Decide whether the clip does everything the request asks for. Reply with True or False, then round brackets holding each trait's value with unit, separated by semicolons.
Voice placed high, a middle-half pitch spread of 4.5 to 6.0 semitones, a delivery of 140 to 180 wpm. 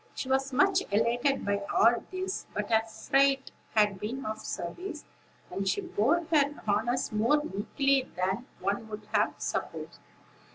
True (245 Hz; 5.3 semitones; 150 wpm)